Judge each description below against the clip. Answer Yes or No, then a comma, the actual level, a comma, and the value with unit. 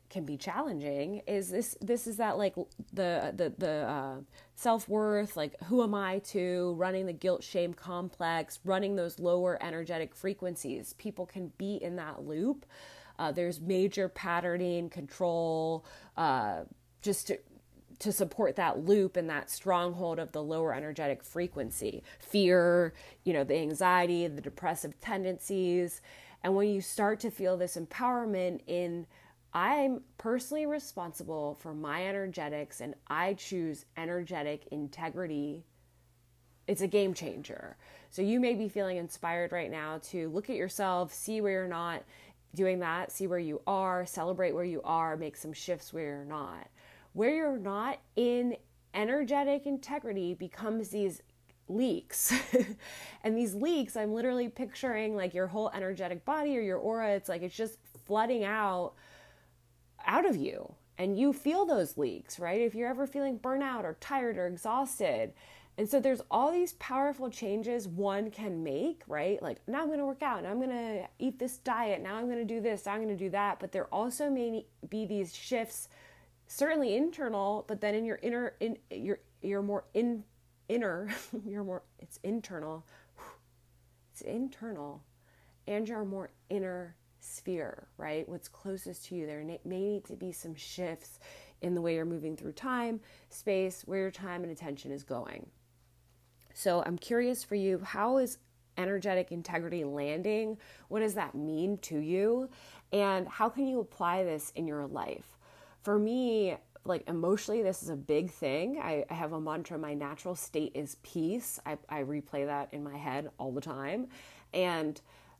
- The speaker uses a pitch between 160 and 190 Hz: Yes, medium, 185 Hz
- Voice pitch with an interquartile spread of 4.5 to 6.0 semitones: Yes, average, 5.0 semitones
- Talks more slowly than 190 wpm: Yes, average, 165 wpm